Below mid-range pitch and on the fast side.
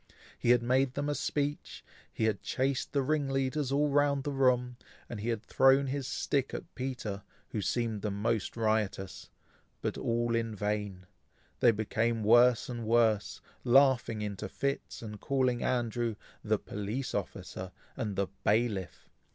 No: low, 120 Hz; average, 155 wpm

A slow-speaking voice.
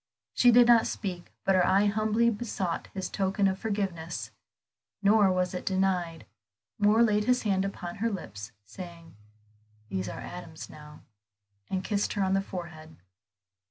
No: average, 155 wpm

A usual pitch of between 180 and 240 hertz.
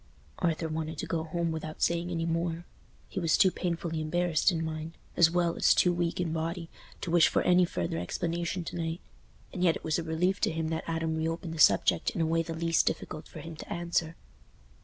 No: medium, 165 Hz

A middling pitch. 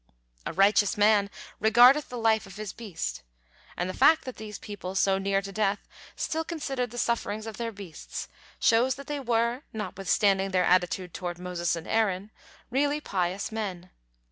No: high, 210 Hz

